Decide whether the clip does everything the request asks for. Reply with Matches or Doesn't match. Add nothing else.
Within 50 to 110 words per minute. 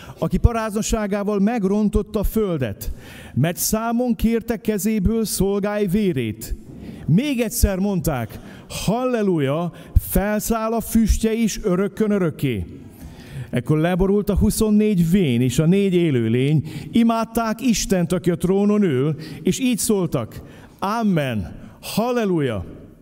Matches